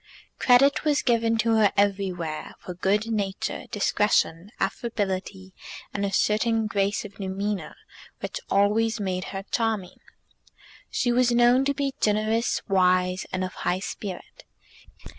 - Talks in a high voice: Yes, high, 205 Hz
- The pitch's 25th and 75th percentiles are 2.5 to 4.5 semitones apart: Yes, average, 3.1 semitones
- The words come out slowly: Yes, slow, 130 wpm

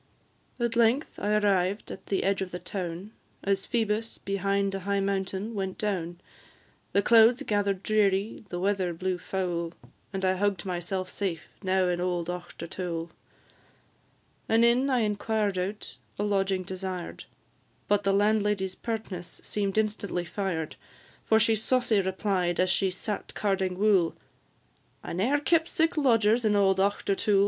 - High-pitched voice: Yes, high, 195 Hz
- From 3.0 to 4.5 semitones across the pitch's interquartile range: No, narrow, 2.4 semitones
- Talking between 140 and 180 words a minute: Yes, average, 145 wpm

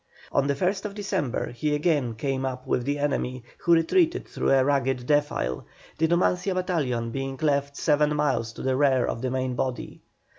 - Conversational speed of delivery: Yes, average, 180 wpm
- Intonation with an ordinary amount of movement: Yes, average, 3.5 semitones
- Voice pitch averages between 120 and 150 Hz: Yes, medium, 140 Hz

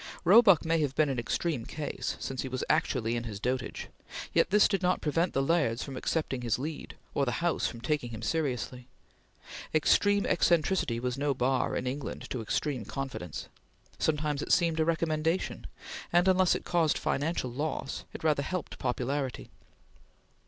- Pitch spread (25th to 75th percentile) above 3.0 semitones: Yes, average, 4.6 semitones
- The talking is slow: No, average, 165 wpm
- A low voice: No, medium, 145 Hz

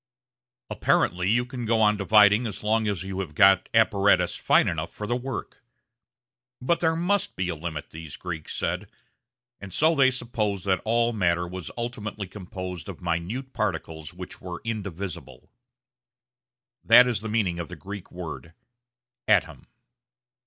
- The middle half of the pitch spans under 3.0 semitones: No, average, 4.4 semitones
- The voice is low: Yes, low, 100 Hz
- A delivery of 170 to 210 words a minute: No, average, 150 wpm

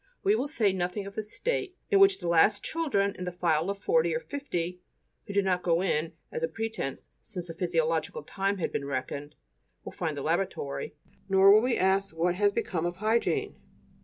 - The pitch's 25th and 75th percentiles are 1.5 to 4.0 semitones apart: No, average, 4.8 semitones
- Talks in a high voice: Yes, high, 195 Hz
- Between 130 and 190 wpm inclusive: No, average, 200 wpm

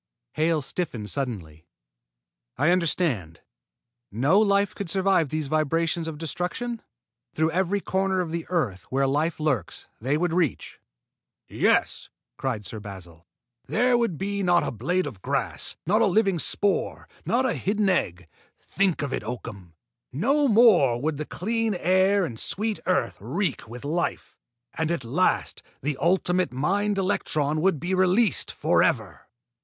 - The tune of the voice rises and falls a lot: Yes, wide, 6.1 semitones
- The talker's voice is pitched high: No, medium, 170 Hz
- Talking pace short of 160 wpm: Yes, average, 150 wpm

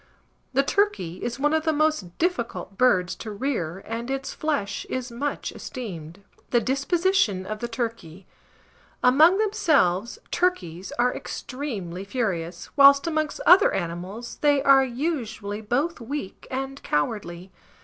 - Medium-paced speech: No, slow, 130 wpm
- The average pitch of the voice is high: Yes, high, 240 Hz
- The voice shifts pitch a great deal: Yes, wide, 7.0 semitones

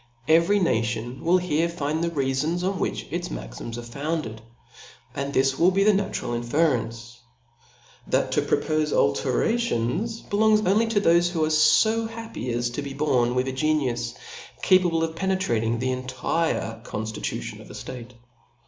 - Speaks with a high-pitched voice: No, medium, 150 Hz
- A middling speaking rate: Yes, average, 155 wpm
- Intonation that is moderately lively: No, wide, 6.8 semitones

